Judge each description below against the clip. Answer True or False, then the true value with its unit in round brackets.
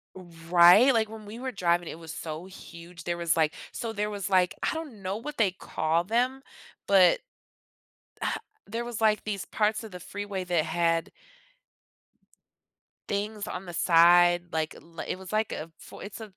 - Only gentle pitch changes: False (3.9 semitones)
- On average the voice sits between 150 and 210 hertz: True (190 Hz)